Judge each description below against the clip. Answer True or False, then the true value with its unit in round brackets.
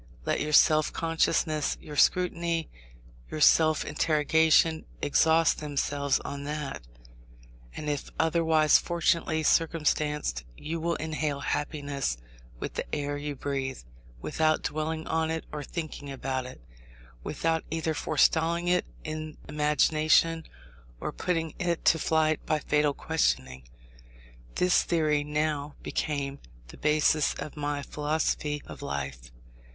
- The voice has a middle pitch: True (155 Hz)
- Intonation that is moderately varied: False (1.9 semitones)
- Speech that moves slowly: True (120 wpm)